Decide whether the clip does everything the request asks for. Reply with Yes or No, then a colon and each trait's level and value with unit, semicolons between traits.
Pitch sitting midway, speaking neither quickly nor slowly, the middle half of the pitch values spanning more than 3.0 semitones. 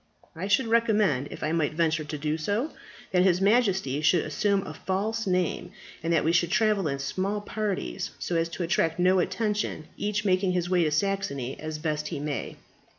Yes: medium, 180 Hz; average, 195 wpm; average, 4.6 semitones